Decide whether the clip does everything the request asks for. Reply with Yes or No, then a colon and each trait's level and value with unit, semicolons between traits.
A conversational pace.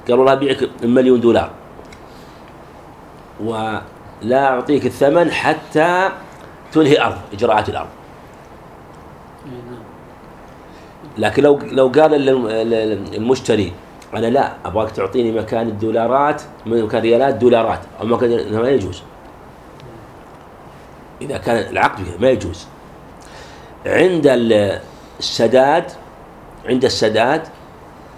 Yes: average, 85 wpm